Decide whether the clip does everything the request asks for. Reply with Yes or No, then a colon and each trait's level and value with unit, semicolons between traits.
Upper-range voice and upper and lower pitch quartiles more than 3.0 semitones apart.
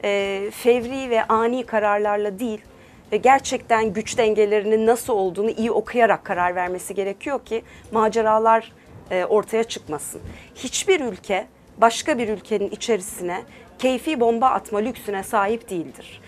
No: high, 220 Hz; narrow, 2.4 semitones